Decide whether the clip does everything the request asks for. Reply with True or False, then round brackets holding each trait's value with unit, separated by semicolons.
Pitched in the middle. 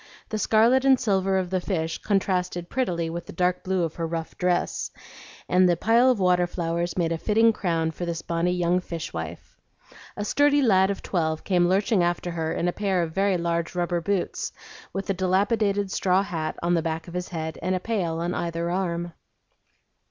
True (180 Hz)